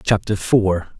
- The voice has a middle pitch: No, very low, 95 Hz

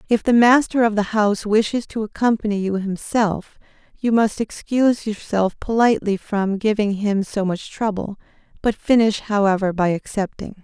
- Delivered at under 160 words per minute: Yes, average, 150 wpm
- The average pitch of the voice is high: Yes, high, 210 Hz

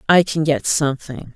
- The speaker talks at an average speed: Yes, average, 175 wpm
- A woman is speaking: Yes, female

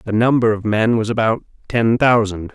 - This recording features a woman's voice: No, male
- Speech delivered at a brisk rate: No, average, 190 wpm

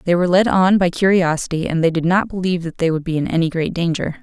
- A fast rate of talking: Yes, fast, 270 wpm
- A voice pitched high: No, medium, 175 Hz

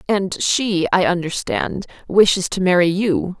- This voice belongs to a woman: Yes, female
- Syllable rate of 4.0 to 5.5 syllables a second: Yes, 4.1 syllables/s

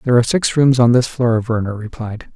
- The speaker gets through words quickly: Yes, fast, 230 wpm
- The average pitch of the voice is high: No, low, 120 Hz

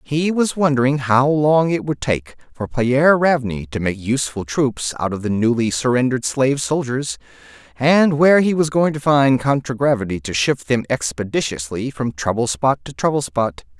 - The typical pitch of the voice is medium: No, low, 130 Hz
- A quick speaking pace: No, average, 175 wpm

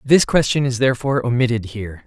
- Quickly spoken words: No, average, 175 wpm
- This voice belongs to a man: Yes, male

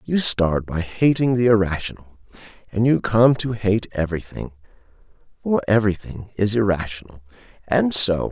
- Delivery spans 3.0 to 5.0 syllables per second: Yes, 4.9 syllables/s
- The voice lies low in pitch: Yes, low, 105 Hz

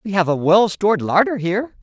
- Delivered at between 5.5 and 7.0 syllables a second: Yes, 5.9 syllables/s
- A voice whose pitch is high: Yes, high, 195 Hz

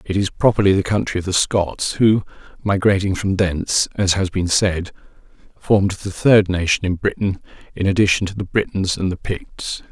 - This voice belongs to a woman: No, male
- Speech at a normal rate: Yes, average, 180 wpm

